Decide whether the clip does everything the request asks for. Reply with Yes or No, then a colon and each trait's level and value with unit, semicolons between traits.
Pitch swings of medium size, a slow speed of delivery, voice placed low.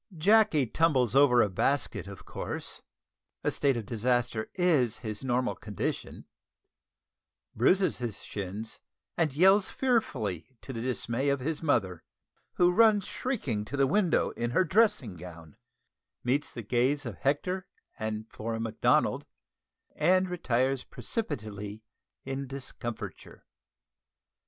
No: wide, 6.9 semitones; slow, 125 wpm; low, 130 Hz